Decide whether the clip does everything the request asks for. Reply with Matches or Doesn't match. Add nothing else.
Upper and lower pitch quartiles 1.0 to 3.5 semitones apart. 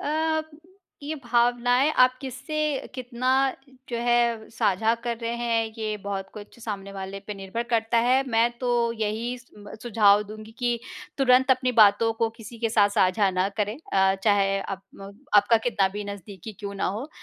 Matches